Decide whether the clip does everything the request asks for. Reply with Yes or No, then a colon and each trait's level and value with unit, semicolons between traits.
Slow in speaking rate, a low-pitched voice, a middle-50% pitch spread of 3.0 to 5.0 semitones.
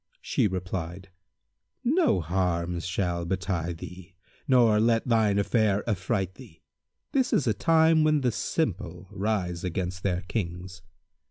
Yes: slow, 125 wpm; very low, 95 Hz; average, 4.3 semitones